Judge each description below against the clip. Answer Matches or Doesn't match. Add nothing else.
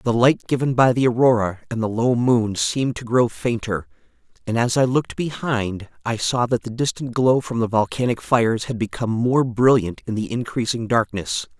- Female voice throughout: Doesn't match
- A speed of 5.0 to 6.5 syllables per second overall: Matches